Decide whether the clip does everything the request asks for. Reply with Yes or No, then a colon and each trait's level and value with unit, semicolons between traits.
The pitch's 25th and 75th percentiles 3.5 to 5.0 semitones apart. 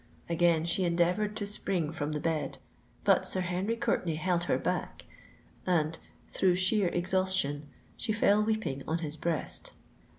No: average, 2.9 semitones